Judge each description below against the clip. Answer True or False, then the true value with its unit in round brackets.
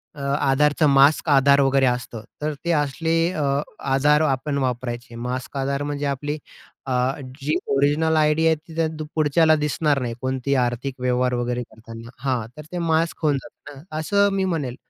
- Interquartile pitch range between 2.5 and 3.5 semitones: True (3.1 semitones)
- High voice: False (140 Hz)